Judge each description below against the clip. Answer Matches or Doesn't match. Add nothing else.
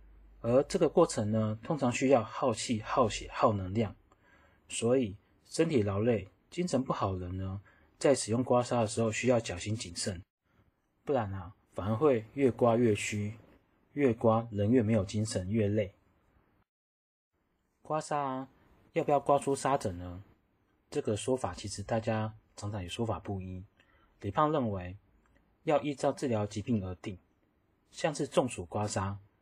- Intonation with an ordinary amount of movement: Matches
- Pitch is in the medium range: Doesn't match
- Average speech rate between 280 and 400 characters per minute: Doesn't match